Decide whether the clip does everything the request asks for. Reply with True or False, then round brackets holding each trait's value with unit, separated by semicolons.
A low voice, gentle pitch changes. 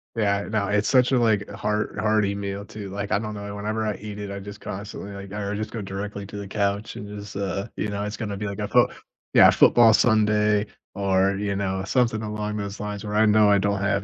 True (105 Hz; 1.0 semitones)